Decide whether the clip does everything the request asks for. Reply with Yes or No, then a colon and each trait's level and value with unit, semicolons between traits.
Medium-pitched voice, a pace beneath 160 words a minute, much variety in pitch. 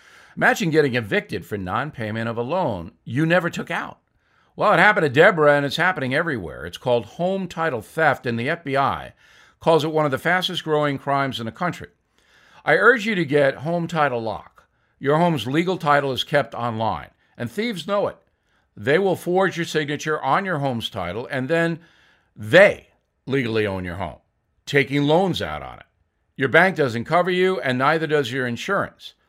No: medium, 145 Hz; average, 185 wpm; wide, 5.7 semitones